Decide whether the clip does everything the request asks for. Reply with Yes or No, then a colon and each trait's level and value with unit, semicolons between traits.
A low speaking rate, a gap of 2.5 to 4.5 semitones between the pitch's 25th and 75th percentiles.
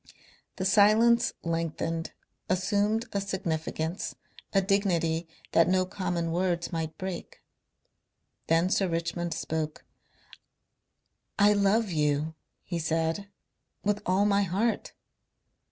Yes: slow, 105 wpm; average, 3.3 semitones